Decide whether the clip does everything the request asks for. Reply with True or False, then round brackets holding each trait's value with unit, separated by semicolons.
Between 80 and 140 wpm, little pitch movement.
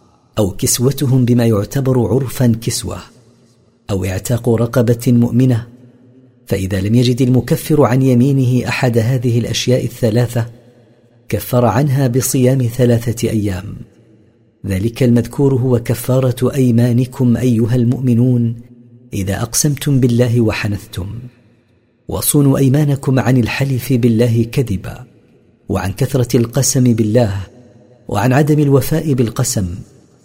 True (100 wpm; 1.8 semitones)